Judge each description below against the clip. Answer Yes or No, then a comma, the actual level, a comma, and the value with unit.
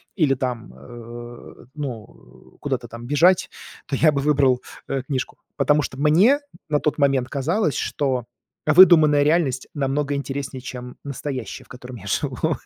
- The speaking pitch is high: No, medium, 140 Hz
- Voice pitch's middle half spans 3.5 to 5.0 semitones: No, average, 3.1 semitones